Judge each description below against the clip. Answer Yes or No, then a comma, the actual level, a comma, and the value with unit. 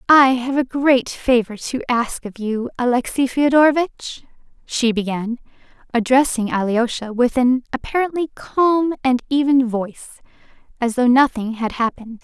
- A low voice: No, very high, 250 Hz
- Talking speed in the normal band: No, slow, 130 wpm